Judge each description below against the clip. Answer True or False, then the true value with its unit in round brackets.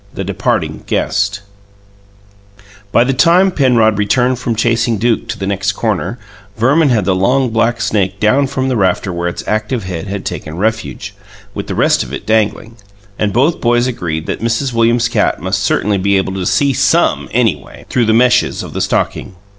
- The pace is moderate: True (185 wpm)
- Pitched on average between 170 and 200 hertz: False (115 Hz)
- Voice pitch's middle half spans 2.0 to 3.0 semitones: False (3.8 semitones)